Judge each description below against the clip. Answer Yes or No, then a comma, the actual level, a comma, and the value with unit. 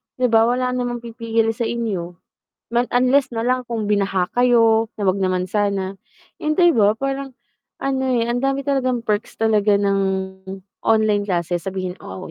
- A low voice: No, high, 225 Hz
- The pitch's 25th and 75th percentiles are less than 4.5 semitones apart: Yes, average, 3.8 semitones